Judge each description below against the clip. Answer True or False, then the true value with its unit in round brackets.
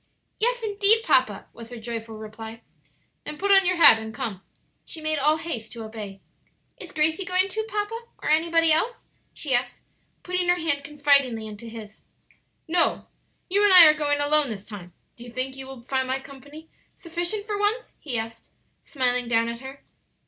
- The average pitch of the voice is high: True (285 Hz)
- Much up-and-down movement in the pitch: True (7.1 semitones)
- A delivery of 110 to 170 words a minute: False (185 wpm)